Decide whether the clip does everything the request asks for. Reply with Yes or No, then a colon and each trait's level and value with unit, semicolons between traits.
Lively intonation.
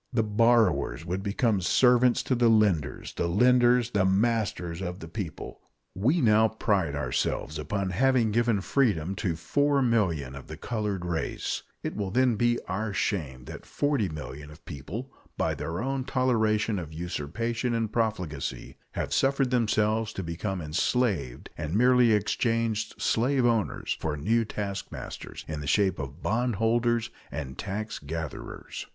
Yes: wide, 5.9 semitones